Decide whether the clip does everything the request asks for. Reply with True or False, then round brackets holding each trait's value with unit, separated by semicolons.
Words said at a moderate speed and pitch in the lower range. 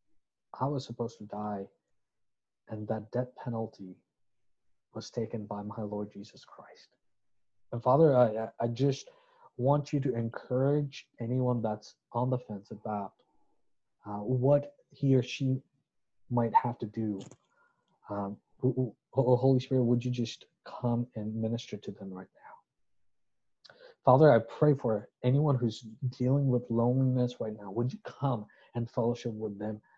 True (145 wpm; 120 Hz)